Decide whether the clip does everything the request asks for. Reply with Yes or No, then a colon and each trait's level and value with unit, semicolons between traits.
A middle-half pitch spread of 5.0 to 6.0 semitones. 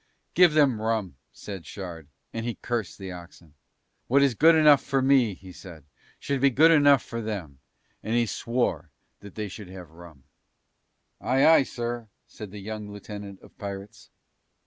Yes: wide, 5.6 semitones